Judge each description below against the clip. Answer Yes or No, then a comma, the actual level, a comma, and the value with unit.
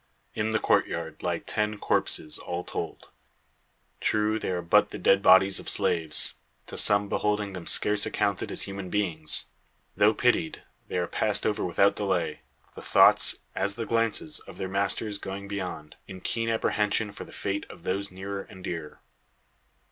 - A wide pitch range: No, narrow, 2.5 semitones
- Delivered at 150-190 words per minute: Yes, average, 165 wpm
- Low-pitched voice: Yes, low, 100 Hz